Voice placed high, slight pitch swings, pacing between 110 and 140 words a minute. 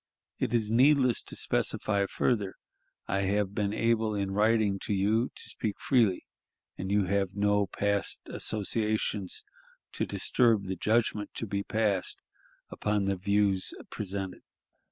No: low, 105 Hz; narrow, 2.0 semitones; slow, 135 wpm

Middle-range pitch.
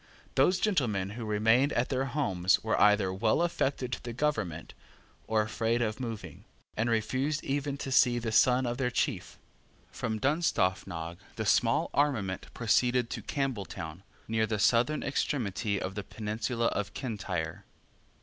No: low, 115 Hz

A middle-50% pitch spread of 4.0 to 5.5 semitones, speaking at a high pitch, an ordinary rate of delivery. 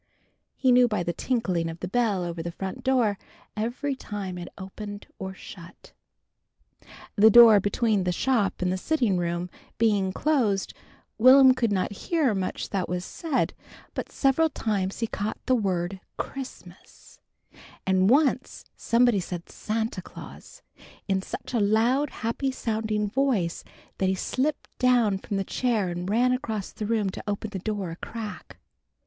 Yes: average, 4.5 semitones; high, 210 Hz; average, 155 wpm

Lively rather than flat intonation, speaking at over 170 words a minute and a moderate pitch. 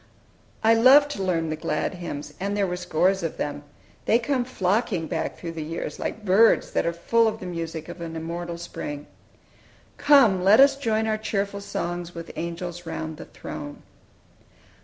No: average, 4.7 semitones; average, 180 wpm; medium, 180 Hz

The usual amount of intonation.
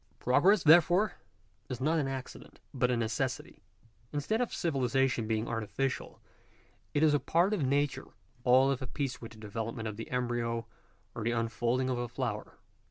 Yes: average, 3.7 semitones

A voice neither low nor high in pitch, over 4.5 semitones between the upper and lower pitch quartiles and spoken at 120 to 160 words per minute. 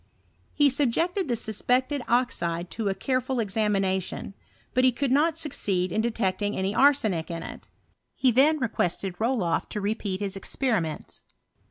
No: high, 220 Hz; wide, 5.4 semitones; average, 145 wpm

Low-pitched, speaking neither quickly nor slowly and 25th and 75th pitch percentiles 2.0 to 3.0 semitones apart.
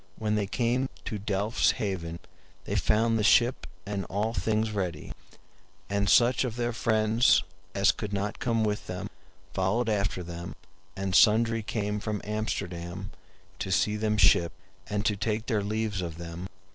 Yes: low, 105 Hz; average, 160 wpm; narrow, 2.4 semitones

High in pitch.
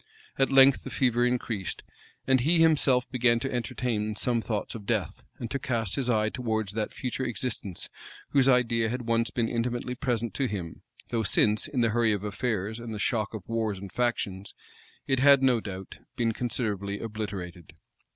No: low, 115 Hz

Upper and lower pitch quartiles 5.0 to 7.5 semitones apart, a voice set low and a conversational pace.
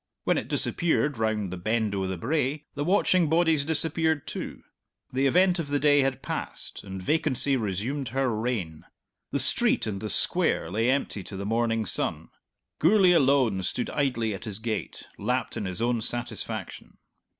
Yes: average, 5.3 semitones; low, 125 Hz; average, 170 wpm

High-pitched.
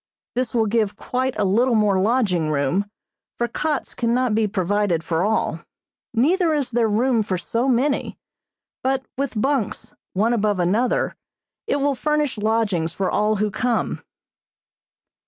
Yes: high, 225 Hz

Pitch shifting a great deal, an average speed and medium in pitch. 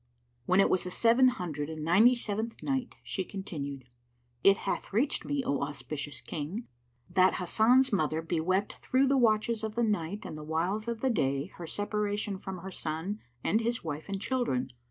No: wide, 6.1 semitones; average, 180 wpm; high, 195 Hz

